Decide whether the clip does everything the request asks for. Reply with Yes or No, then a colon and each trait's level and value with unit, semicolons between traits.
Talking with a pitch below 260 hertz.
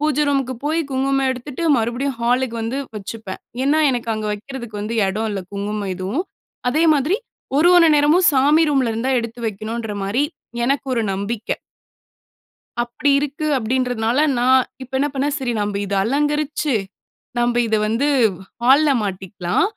Yes: very high, 250 Hz